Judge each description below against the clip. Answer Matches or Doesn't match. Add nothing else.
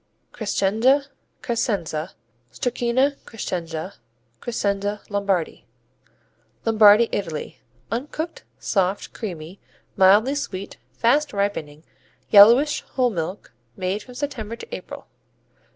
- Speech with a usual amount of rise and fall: Matches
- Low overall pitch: Doesn't match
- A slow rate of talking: Matches